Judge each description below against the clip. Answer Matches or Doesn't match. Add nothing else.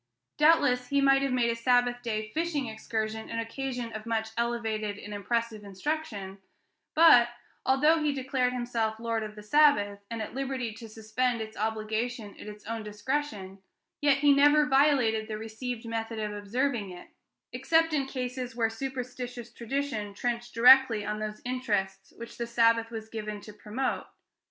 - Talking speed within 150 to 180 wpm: Matches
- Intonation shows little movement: Doesn't match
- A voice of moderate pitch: Doesn't match